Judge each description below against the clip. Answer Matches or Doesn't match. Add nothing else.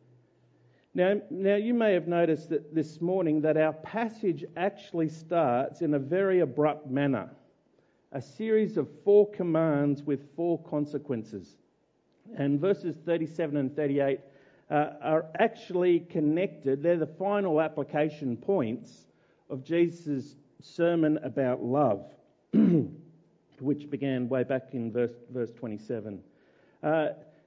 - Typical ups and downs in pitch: Matches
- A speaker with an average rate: Doesn't match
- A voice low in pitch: Doesn't match